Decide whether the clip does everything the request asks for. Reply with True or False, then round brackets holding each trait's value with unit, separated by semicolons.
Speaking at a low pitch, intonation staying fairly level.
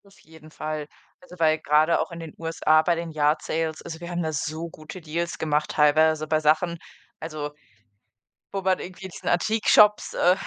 False (160 Hz; 1.8 semitones)